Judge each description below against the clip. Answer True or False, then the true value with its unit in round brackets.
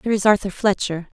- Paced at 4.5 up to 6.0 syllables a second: False (6.9 syllables/s)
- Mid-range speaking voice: False (200 Hz)